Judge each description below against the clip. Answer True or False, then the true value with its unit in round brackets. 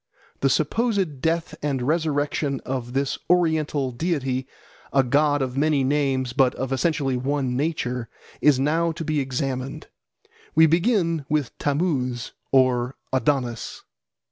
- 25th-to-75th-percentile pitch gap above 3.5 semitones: False (3.2 semitones)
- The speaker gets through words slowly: True (125 wpm)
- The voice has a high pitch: False (140 Hz)